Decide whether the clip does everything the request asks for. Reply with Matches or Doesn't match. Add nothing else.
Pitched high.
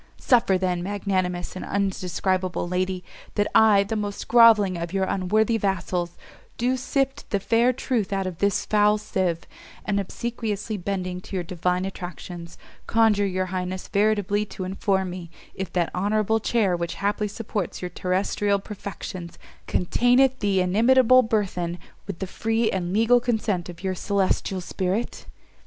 Matches